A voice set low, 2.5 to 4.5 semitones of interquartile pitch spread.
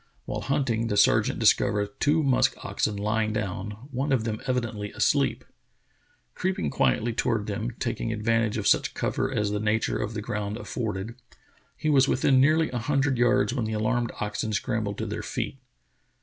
Yes: low, 110 Hz; average, 3.5 semitones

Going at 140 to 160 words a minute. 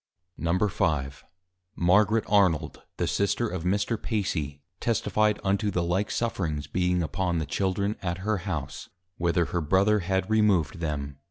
Yes: average, 145 wpm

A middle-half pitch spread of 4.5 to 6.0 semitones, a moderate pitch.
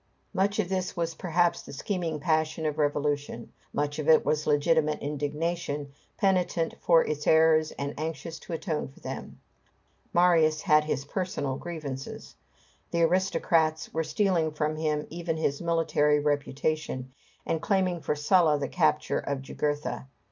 No: narrow, 2.5 semitones; medium, 155 Hz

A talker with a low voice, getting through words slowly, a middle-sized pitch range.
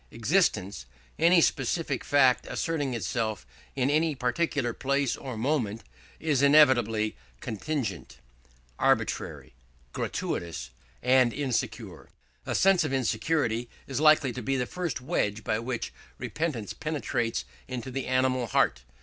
Yes: low, 130 Hz; slow, 120 wpm; average, 4.3 semitones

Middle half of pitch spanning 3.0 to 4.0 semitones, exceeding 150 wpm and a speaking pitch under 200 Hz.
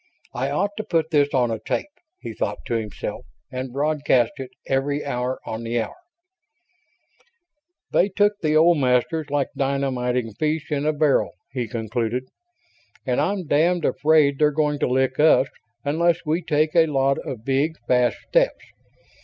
Yes: average, 3.7 semitones; average, 160 wpm; medium, 140 Hz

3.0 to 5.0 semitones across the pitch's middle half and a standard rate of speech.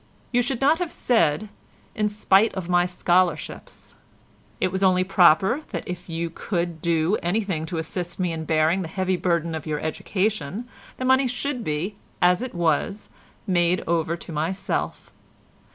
Yes: average, 4.0 semitones; average, 160 wpm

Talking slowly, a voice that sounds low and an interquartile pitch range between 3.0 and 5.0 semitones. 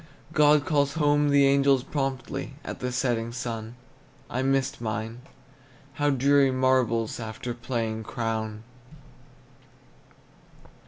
Yes: slow, 105 wpm; low, 130 Hz; average, 3.4 semitones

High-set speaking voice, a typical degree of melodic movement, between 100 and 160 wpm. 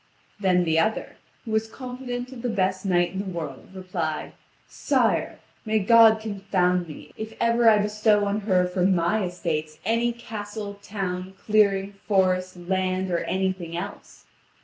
Yes: high, 195 Hz; average, 3.2 semitones; average, 150 wpm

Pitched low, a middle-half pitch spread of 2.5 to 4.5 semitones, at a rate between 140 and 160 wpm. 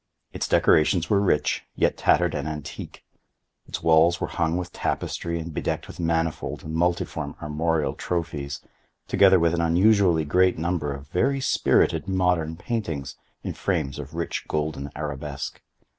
Yes: very low, 80 Hz; average, 2.8 semitones; average, 145 wpm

